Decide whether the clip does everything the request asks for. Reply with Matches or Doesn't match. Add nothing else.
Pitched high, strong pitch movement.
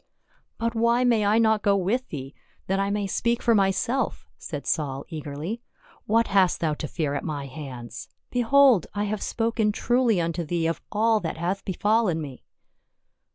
Matches